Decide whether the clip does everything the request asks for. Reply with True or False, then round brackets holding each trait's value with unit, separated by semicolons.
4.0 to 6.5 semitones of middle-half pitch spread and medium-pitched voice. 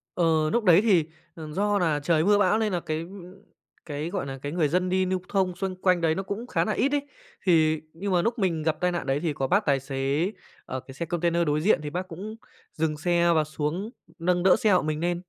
False (3.5 semitones; 175 Hz)